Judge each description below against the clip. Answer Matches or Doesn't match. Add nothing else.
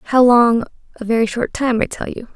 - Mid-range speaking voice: Doesn't match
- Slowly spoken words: Doesn't match